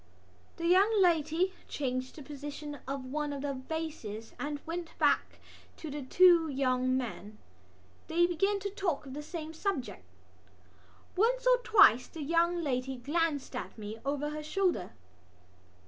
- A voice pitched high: Yes, very high, 300 Hz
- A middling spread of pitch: Yes, average, 4.5 semitones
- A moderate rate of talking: Yes, average, 145 wpm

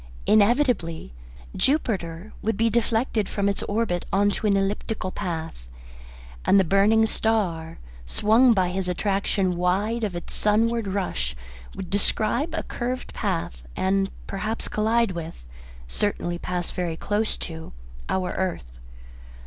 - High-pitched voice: Yes, high, 200 Hz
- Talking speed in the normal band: No, slow, 130 wpm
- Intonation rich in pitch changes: No, average, 3.9 semitones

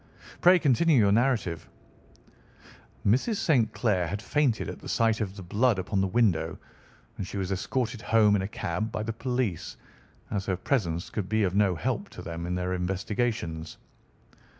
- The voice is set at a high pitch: No, low, 105 Hz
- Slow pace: No, average, 175 wpm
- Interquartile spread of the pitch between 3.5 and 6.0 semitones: Yes, average, 4.2 semitones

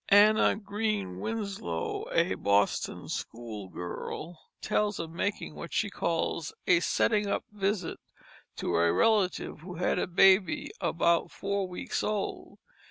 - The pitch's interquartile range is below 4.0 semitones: No, average, 4.5 semitones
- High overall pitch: No, medium, 180 Hz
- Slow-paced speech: Yes, slow, 125 wpm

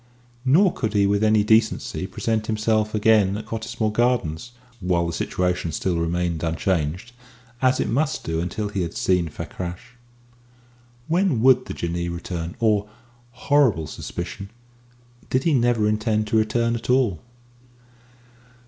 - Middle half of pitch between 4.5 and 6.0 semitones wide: Yes, average, 4.8 semitones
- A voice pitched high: No, low, 105 Hz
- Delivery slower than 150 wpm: Yes, average, 140 wpm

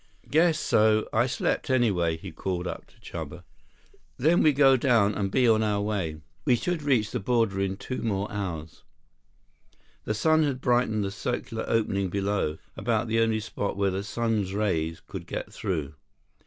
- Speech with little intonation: No, average, 3.8 semitones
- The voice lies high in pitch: No, low, 110 Hz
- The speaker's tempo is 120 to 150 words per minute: No, average, 170 wpm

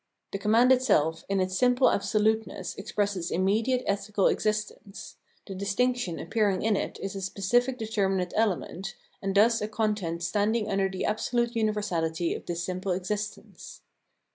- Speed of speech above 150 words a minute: No, average, 145 wpm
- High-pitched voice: Yes, high, 205 Hz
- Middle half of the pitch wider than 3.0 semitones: No, average, 2.7 semitones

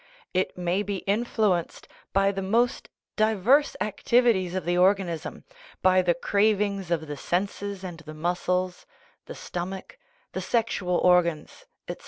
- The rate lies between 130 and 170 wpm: Yes, slow, 135 wpm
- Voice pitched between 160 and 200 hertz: Yes, medium, 185 Hz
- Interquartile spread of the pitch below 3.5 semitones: Yes, narrow, 2.6 semitones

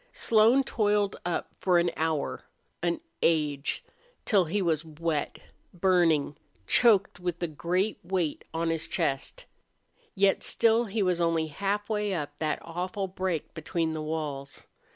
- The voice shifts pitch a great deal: No, average, 3.8 semitones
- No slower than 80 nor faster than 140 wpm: Yes, slow, 135 wpm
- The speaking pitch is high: No, medium, 175 Hz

